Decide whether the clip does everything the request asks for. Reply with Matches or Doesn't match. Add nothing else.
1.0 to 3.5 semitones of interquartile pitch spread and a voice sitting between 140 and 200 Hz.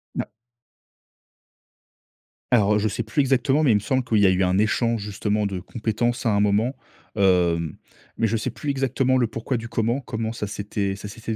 Doesn't match